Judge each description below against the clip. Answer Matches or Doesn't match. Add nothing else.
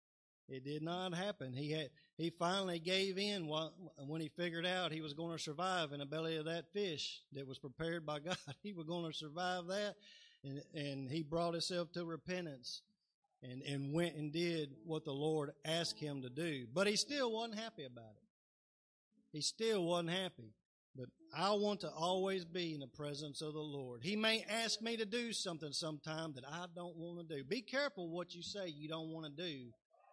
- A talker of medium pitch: Matches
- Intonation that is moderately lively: Matches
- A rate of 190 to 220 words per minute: Matches